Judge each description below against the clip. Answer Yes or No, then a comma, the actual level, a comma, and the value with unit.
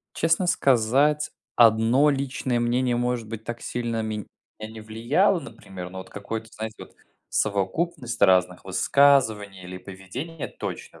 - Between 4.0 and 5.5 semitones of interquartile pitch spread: Yes, average, 4.8 semitones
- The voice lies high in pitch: No, low, 115 Hz